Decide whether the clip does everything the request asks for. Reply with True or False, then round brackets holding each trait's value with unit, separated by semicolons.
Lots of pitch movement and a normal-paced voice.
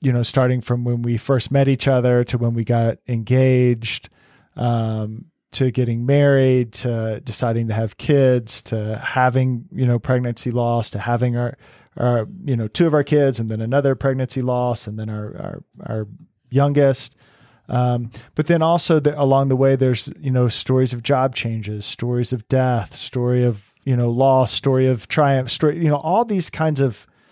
False (2.6 semitones; 185 wpm)